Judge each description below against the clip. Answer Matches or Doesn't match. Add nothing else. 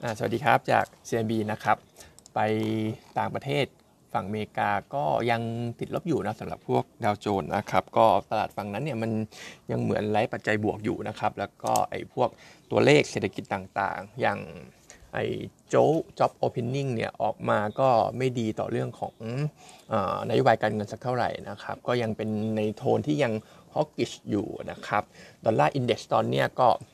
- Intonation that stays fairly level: Matches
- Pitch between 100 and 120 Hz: Matches